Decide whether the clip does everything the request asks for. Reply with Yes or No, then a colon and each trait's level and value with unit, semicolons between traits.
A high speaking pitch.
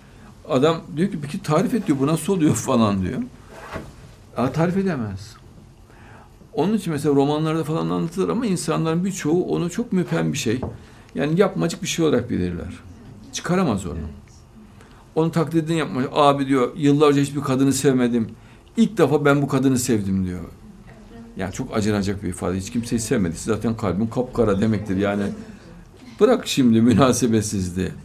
No: low, 130 Hz